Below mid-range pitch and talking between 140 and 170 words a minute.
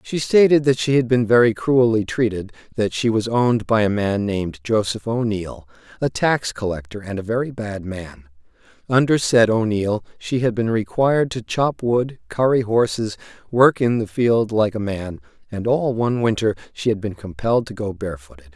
No: low, 110 Hz; average, 185 wpm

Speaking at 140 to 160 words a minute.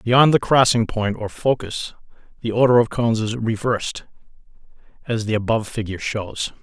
Yes: average, 155 wpm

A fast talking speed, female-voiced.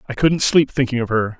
No: fast, 260 wpm; male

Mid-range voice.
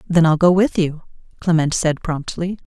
Yes: medium, 165 Hz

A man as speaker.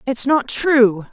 No: female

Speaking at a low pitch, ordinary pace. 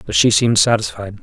Yes: low, 100 Hz; average, 195 wpm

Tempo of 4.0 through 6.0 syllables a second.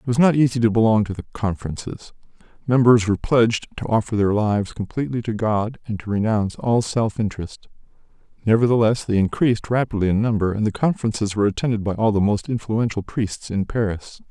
No: 6.2 syllables/s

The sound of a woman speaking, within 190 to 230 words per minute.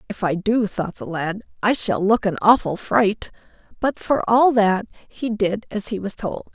Yes: female; average, 200 wpm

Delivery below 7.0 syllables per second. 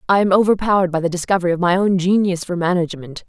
No: 7.4 syllables/s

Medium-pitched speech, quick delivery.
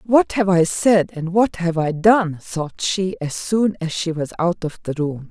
Yes: medium, 180 Hz; fast, 225 wpm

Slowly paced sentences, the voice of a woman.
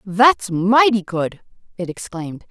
Yes: slow, 120 wpm; female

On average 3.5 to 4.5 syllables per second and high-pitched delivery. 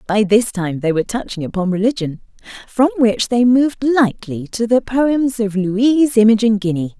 No: 5.0 syllables/s; high, 225 Hz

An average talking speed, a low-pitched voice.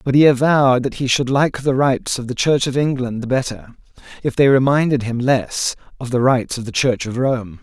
No: fast, 220 wpm; low, 130 Hz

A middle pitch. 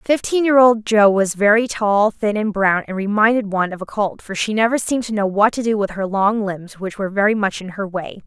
No: high, 210 Hz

